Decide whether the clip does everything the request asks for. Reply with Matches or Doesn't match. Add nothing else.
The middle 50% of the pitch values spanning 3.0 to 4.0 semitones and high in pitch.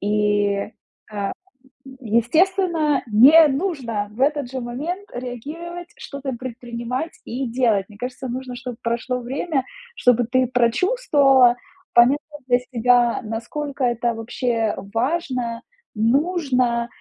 Matches